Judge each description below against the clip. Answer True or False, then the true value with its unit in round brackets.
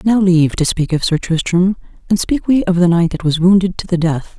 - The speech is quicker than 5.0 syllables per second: True (5.5 syllables/s)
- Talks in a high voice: False (180 Hz)